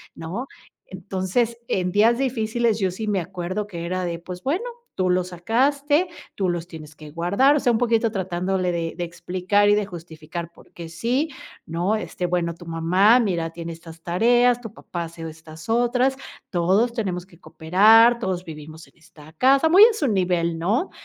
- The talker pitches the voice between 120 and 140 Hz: No, medium, 185 Hz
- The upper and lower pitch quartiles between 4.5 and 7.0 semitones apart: Yes, average, 5.2 semitones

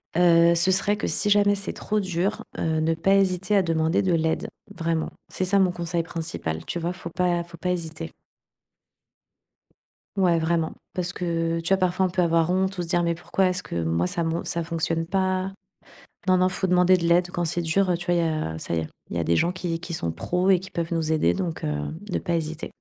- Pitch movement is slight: Yes, narrow, 2.0 semitones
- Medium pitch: Yes, medium, 170 Hz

